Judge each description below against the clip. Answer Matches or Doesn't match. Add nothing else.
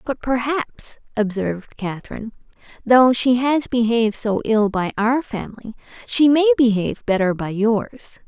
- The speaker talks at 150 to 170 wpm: Doesn't match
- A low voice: Doesn't match